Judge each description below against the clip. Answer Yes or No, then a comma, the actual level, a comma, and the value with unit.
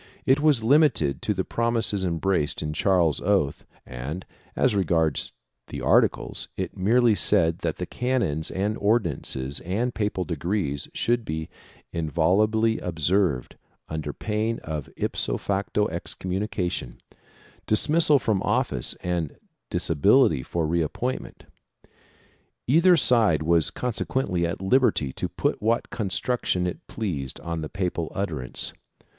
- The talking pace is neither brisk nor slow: No, slow, 130 wpm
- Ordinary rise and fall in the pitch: No, wide, 5.9 semitones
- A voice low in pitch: Yes, very low, 95 Hz